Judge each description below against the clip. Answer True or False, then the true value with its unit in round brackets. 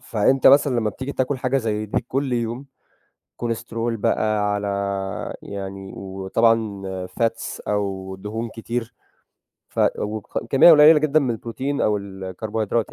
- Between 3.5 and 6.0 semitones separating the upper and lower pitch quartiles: True (3.8 semitones)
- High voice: False (115 Hz)